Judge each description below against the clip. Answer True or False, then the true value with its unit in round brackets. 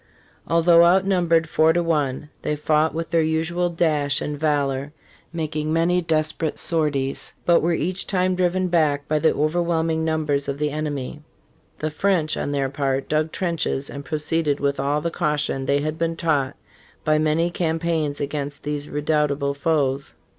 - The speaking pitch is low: False (155 Hz)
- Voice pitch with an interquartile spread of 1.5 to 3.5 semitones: True (2.4 semitones)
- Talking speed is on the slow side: False (160 wpm)